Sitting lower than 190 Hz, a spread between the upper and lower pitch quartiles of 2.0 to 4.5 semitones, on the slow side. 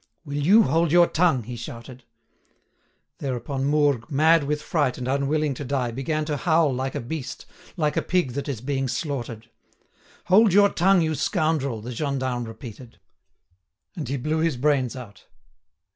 No: medium, 140 Hz; average, 3.9 semitones; average, 160 wpm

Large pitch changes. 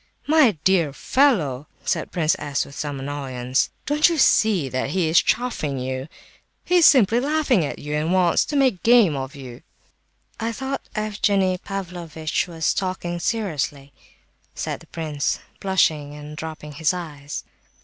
Yes: wide, 6.7 semitones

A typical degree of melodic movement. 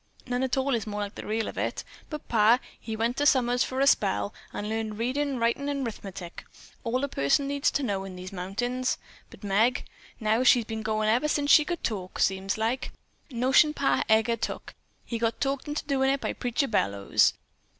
Yes: average, 4.0 semitones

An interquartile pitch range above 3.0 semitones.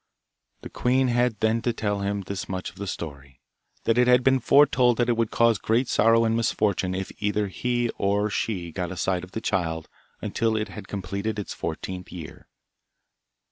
Yes: average, 3.8 semitones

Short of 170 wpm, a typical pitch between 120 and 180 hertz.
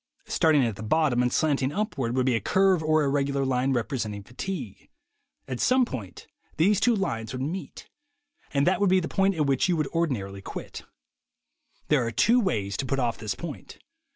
No: average, 200 wpm; medium, 140 Hz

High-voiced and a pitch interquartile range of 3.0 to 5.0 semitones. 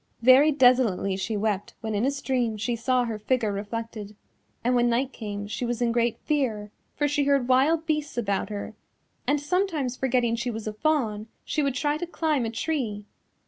Yes: high, 240 Hz; average, 4.4 semitones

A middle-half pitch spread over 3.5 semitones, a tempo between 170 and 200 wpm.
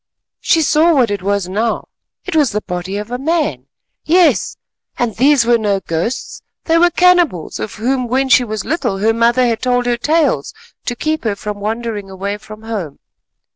Yes: average, 5.0 semitones; average, 180 wpm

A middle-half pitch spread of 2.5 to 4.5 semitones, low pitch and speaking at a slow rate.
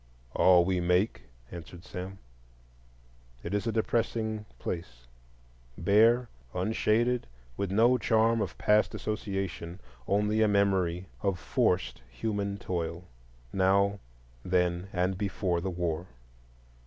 Yes: average, 3.5 semitones; very low, 95 Hz; slow, 105 wpm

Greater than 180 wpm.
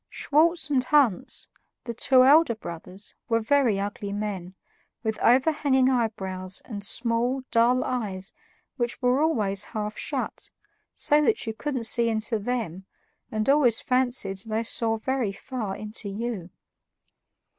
No: slow, 135 wpm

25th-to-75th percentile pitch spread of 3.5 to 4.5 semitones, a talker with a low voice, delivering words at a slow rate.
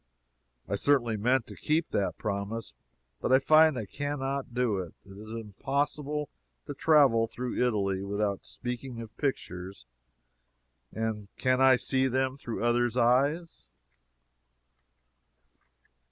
Yes: average, 4.2 semitones; low, 125 Hz; slow, 125 wpm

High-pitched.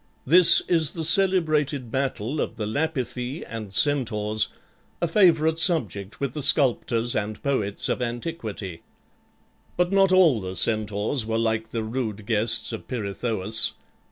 No: low, 120 Hz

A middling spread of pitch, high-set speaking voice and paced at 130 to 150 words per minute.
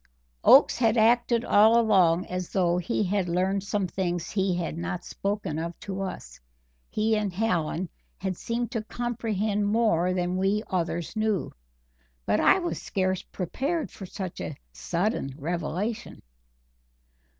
Yes: average, 3.6 semitones; high, 195 Hz; average, 140 wpm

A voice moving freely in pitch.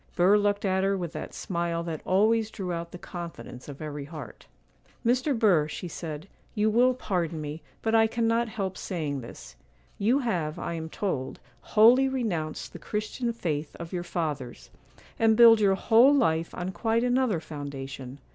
Yes: wide, 6.0 semitones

